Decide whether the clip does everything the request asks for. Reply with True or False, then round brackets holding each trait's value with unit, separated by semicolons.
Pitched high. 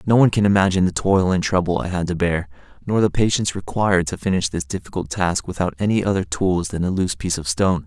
False (95 Hz)